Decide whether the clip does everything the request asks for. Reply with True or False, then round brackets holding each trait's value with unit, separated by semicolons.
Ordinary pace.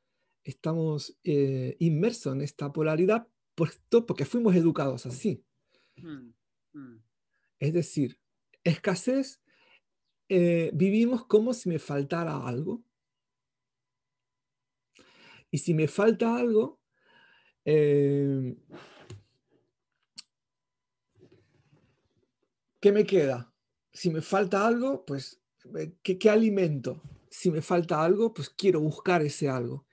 False (90 wpm)